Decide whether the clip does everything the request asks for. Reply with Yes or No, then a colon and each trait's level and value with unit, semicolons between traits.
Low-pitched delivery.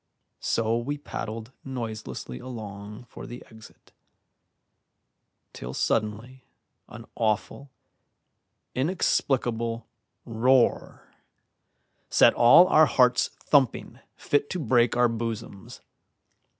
Yes: low, 120 Hz